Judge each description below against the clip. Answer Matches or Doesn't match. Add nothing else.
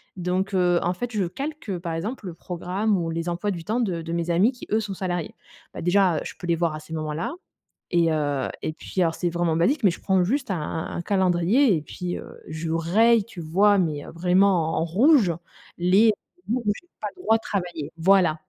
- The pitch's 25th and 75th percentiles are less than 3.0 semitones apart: Doesn't match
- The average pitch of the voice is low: Doesn't match